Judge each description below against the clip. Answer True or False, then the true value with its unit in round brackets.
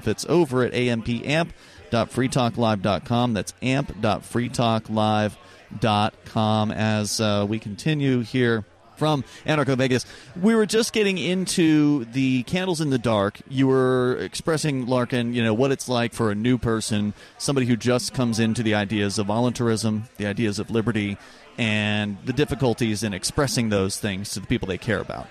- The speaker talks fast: False (150 wpm)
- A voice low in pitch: True (120 Hz)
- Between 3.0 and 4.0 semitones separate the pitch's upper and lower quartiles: True (3.7 semitones)